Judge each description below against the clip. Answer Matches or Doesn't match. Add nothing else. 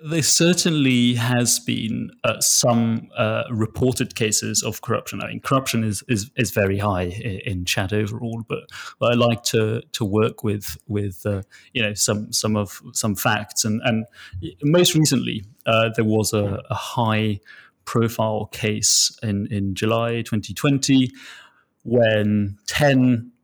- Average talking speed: Matches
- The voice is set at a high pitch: Doesn't match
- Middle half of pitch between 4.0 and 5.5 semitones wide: Doesn't match